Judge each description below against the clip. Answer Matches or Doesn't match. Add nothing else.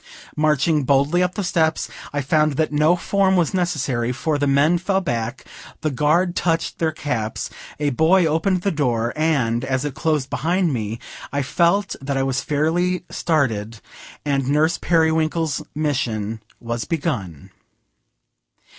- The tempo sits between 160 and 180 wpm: Doesn't match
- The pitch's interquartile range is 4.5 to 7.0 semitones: Doesn't match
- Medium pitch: Matches